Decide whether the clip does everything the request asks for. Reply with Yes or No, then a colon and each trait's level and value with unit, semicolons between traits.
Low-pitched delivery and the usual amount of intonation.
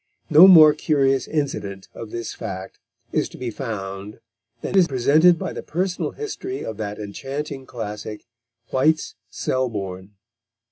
No: low, 130 Hz; wide, 6.7 semitones